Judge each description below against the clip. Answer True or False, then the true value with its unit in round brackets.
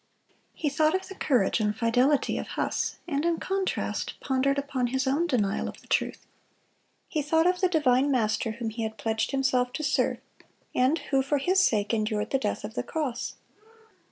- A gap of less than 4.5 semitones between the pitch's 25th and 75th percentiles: False (4.9 semitones)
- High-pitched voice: True (265 Hz)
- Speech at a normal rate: True (185 wpm)